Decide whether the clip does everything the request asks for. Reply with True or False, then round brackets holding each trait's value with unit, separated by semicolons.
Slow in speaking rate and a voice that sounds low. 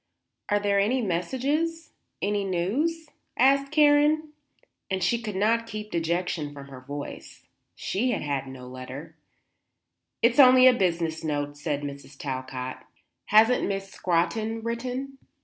False (130 wpm; 200 Hz)